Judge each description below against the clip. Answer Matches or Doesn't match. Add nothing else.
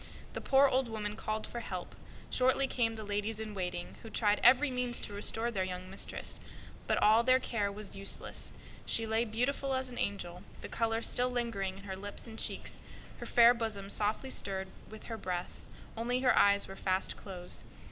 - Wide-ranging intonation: Doesn't match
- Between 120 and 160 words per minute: Doesn't match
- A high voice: Matches